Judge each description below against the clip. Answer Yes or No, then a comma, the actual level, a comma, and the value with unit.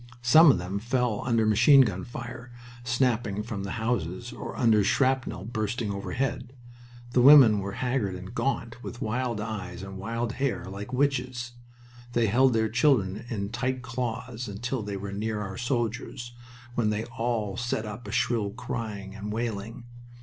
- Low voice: Yes, low, 115 Hz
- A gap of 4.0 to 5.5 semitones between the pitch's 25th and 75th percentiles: No, average, 3.2 semitones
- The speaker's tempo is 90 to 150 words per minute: No, average, 160 wpm